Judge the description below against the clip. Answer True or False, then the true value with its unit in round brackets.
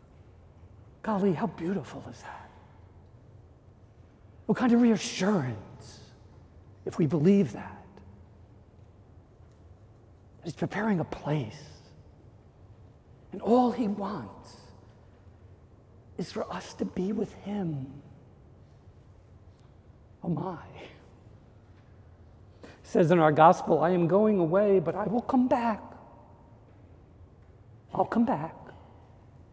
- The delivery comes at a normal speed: False (95 wpm)